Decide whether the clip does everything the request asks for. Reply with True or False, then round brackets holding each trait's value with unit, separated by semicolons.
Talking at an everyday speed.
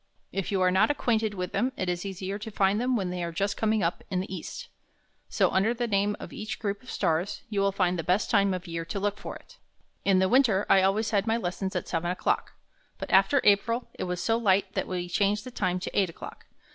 False (245 wpm)